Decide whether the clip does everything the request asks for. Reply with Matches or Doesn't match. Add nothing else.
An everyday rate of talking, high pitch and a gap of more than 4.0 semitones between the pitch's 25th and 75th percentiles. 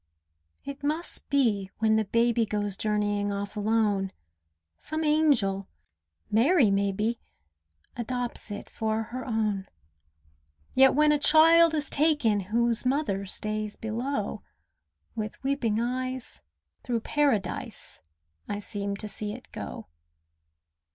Doesn't match